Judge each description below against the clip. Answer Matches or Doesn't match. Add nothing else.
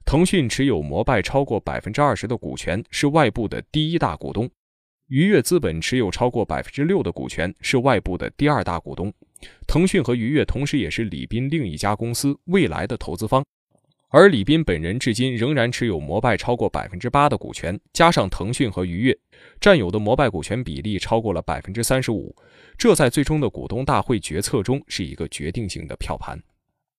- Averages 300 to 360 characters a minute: Matches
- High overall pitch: Doesn't match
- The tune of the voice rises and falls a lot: Matches